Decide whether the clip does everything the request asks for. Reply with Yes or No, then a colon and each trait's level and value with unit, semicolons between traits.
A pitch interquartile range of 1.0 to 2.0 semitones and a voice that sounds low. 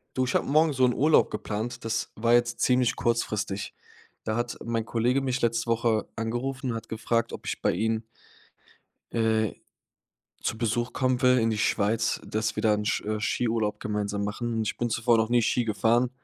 Yes: narrow, 1.7 semitones; low, 115 Hz